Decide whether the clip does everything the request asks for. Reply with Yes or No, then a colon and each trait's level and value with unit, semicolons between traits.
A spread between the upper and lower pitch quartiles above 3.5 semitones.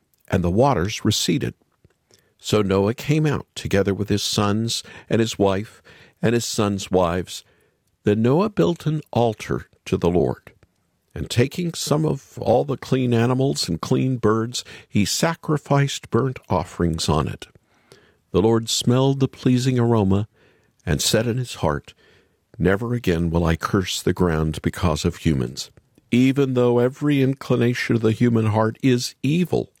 Yes: average, 5.2 semitones